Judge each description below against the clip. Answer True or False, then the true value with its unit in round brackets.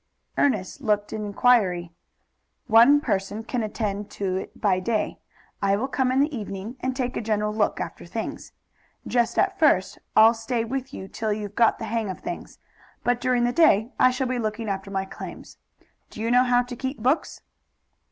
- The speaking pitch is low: False (225 Hz)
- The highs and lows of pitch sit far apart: False (3.5 semitones)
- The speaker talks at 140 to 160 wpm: False (190 wpm)